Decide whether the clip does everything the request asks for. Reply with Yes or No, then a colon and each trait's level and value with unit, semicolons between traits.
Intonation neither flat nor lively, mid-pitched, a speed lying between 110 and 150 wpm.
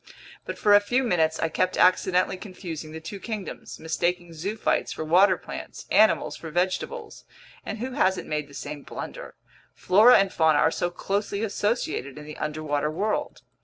No: average, 4.4 semitones; medium, 180 Hz; average, 165 wpm